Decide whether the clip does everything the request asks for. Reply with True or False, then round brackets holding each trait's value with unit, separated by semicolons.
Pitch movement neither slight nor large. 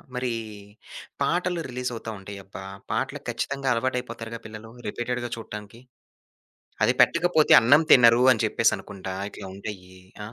True (3.2 semitones)